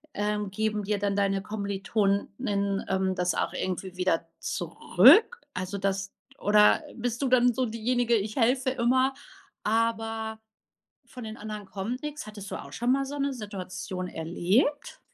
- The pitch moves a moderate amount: Yes, average, 3.9 semitones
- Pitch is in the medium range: No, high, 215 Hz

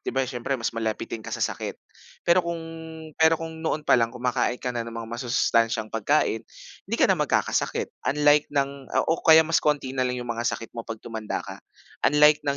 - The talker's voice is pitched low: Yes, low, 130 Hz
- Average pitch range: Yes, average, 4.4 semitones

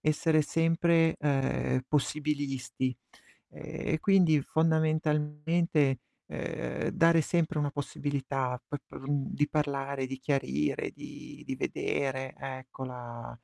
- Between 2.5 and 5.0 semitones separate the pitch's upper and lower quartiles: Yes, average, 2.9 semitones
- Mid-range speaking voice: Yes, medium, 145 Hz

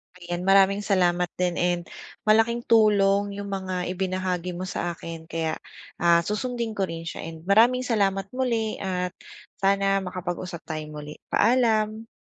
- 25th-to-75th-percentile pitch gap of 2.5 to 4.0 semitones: Yes, average, 3.4 semitones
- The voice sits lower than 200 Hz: Yes, high, 190 Hz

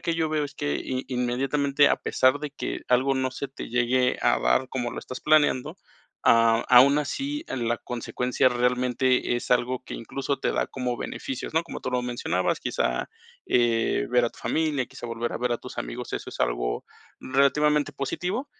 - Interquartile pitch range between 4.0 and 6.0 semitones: No, average, 2.7 semitones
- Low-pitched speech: Yes, low, 125 Hz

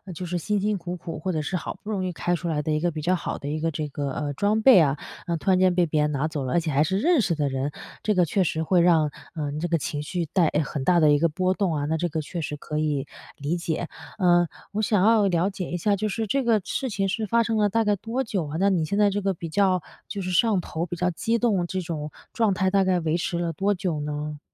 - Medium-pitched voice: Yes, medium, 175 Hz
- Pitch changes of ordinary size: Yes, average, 4.2 semitones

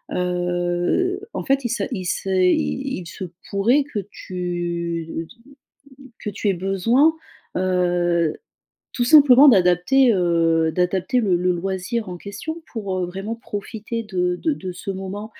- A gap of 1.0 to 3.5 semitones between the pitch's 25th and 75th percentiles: No, average, 4.2 semitones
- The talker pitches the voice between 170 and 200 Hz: Yes, medium, 185 Hz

